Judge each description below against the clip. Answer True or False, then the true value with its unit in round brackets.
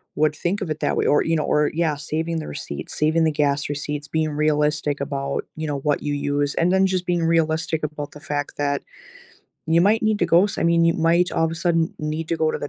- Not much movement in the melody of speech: True (2.2 semitones)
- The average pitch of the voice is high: False (155 Hz)